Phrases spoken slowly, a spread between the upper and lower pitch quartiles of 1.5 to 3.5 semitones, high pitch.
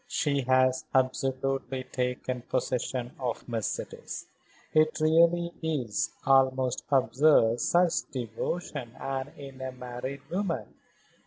No: slow, 100 wpm; average, 2.7 semitones; low, 130 Hz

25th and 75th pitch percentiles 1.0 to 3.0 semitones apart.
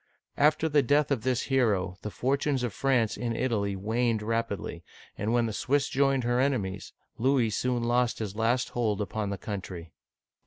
No: average, 3.7 semitones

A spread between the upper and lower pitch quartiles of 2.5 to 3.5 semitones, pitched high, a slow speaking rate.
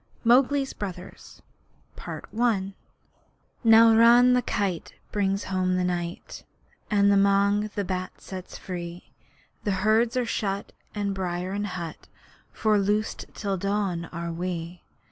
Yes: average, 2.8 semitones; high, 200 Hz; slow, 120 wpm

